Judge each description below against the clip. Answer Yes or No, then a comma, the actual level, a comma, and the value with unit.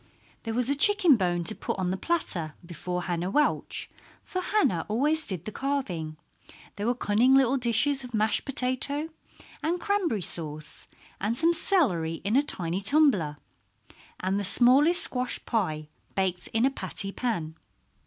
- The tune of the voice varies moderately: No, wide, 7.9 semitones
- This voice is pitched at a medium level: No, high, 225 Hz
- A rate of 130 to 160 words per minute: Yes, average, 155 wpm